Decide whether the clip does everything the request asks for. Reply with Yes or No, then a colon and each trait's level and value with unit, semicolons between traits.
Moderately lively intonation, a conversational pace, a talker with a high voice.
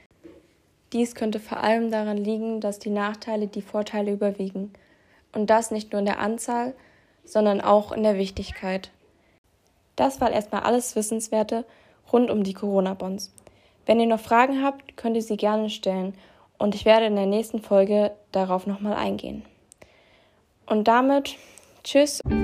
No: narrow, 1.9 semitones; average, 150 wpm; high, 215 Hz